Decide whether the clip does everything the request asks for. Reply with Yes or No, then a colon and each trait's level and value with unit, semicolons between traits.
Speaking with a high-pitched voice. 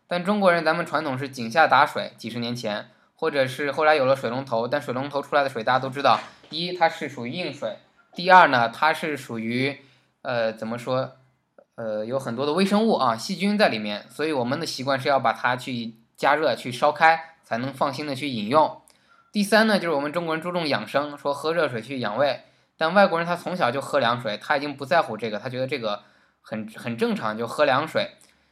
No: medium, 140 Hz